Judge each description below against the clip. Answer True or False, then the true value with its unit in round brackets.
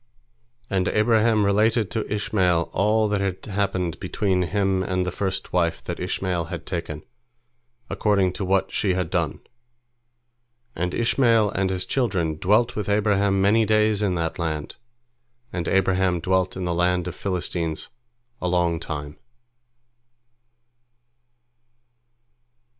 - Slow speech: True (130 wpm)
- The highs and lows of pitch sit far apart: False (2.8 semitones)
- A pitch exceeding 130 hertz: False (95 Hz)